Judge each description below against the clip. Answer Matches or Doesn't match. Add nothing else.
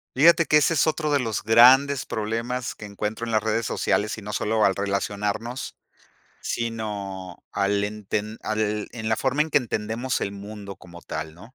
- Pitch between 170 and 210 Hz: Doesn't match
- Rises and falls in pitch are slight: Doesn't match